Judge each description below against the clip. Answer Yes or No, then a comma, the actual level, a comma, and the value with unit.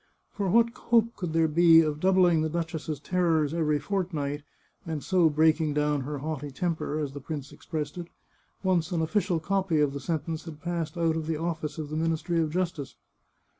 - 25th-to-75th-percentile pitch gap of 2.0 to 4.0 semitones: Yes, narrow, 2.4 semitones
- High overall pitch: No, medium, 160 Hz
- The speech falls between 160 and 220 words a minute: Yes, average, 190 wpm